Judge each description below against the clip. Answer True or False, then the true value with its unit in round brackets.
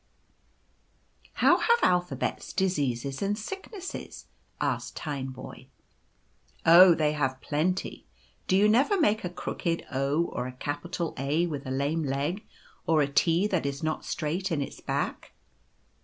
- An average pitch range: True (4.9 semitones)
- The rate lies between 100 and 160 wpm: True (150 wpm)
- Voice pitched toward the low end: False (160 Hz)